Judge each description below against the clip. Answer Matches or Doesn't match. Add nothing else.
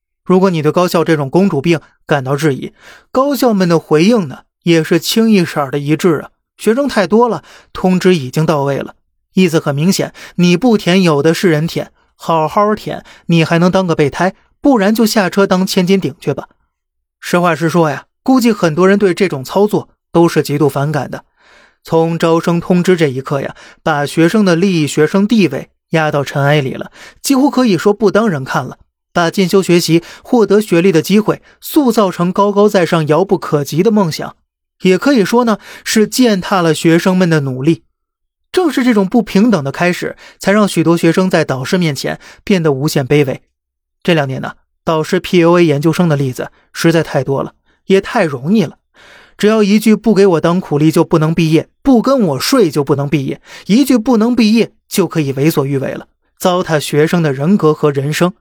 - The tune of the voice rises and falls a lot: Doesn't match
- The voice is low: Doesn't match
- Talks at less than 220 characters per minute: Doesn't match